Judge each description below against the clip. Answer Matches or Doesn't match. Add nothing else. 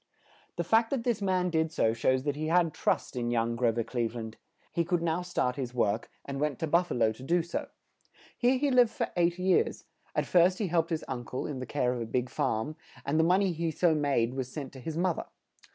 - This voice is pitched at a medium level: Matches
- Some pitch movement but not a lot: Doesn't match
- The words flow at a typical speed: Doesn't match